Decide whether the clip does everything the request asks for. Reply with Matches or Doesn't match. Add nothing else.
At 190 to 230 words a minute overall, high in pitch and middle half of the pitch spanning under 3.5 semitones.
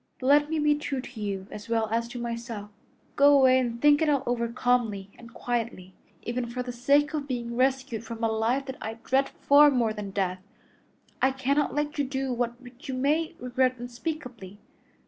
Matches